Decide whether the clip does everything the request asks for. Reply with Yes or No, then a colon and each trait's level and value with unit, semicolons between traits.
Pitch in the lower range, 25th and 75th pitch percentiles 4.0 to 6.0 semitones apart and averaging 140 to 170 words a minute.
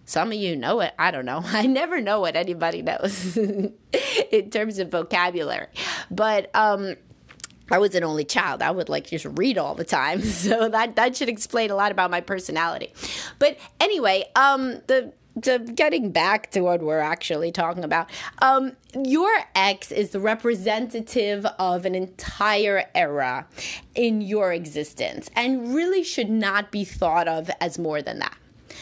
No: high, 205 Hz; average, 4.8 semitones; average, 165 wpm